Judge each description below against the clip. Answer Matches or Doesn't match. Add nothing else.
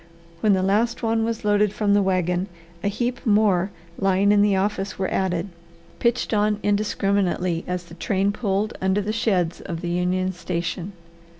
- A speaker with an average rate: Matches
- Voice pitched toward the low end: Doesn't match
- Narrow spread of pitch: Matches